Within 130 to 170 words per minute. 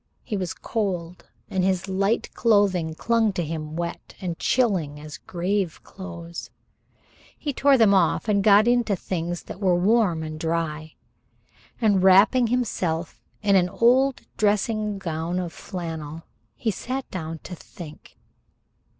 Yes: average, 140 wpm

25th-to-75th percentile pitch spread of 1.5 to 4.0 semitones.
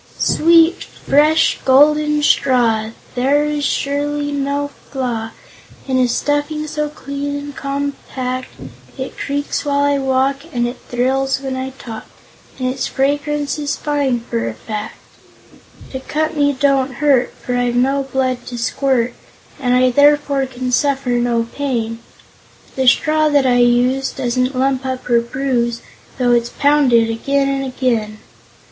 Yes: narrow, 2.5 semitones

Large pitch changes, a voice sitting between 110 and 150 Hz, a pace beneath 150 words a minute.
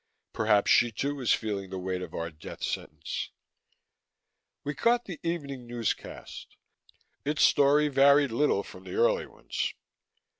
Yes: wide, 5.7 semitones; medium, 140 Hz; average, 140 wpm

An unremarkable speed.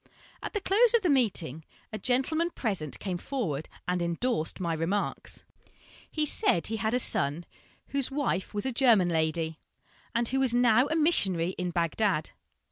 Yes: average, 165 wpm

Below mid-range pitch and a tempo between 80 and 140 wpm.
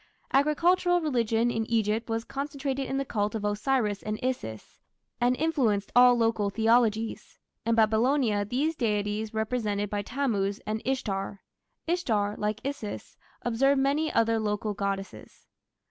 No: high, 225 Hz; slow, 135 wpm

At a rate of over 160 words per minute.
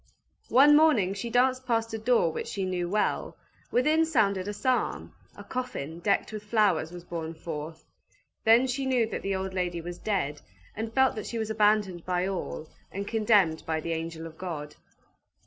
Yes: average, 180 wpm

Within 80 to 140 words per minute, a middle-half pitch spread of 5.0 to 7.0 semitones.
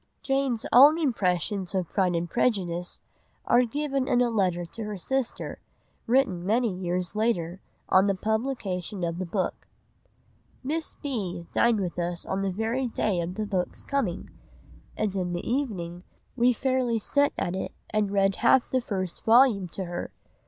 No: average, 160 wpm; average, 5.3 semitones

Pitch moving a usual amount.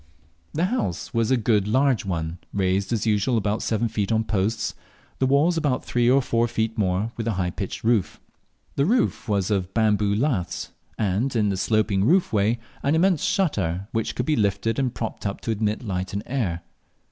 Yes: average, 3.9 semitones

